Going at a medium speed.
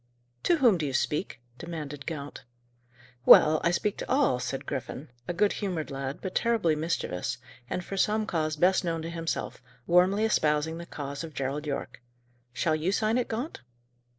Yes: average, 175 wpm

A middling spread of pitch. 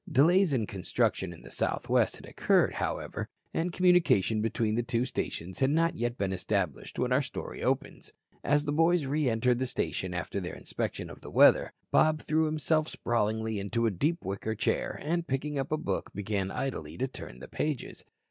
No: wide, 7.1 semitones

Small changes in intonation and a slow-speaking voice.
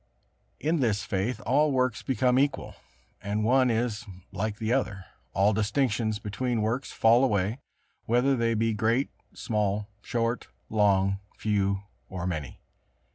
No: average, 3.4 semitones; slow, 130 wpm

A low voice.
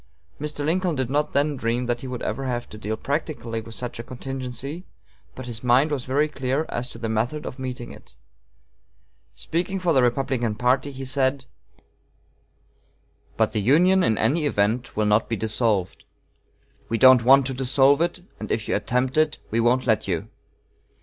Yes: low, 130 Hz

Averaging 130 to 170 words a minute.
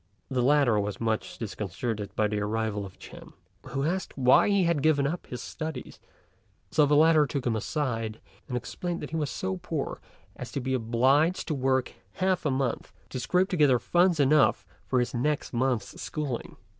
No: average, 185 wpm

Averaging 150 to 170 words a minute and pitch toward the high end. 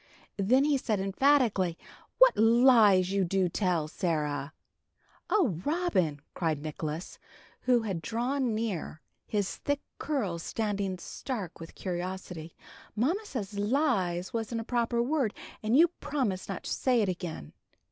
No: slow, 135 wpm; high, 205 Hz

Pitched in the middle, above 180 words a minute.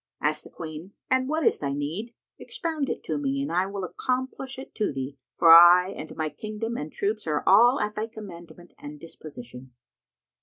Yes: medium, 180 Hz; average, 190 wpm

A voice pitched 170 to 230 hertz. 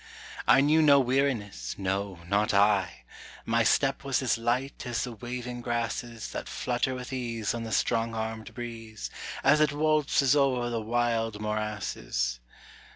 No: low, 120 Hz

